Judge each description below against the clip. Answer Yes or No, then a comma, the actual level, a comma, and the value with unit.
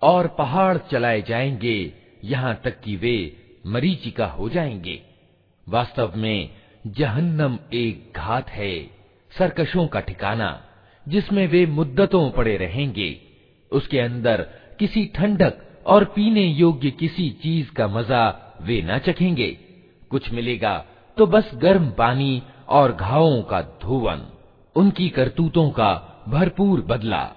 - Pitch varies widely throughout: Yes, wide, 7.2 semitones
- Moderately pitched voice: No, low, 130 Hz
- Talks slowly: No, average, 120 wpm